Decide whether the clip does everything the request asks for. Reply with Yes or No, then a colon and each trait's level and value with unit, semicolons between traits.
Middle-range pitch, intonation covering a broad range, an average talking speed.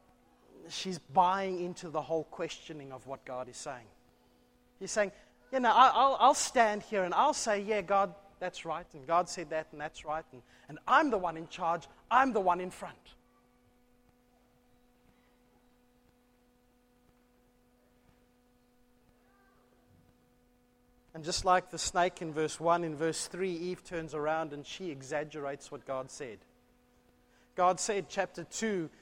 Yes: medium, 165 Hz; wide, 7.4 semitones; average, 145 wpm